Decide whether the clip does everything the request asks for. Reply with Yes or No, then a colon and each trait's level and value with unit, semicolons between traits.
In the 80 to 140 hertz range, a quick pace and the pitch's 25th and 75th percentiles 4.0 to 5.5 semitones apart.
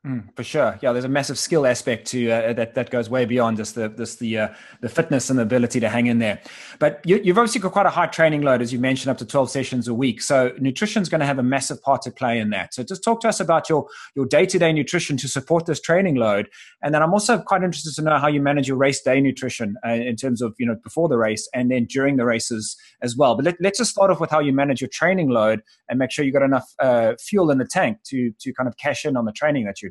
Yes: low, 135 Hz; fast, 290 wpm; average, 4.6 semitones